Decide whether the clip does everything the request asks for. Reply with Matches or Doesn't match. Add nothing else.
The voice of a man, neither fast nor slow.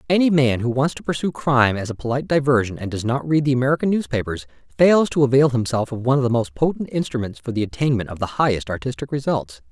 Doesn't match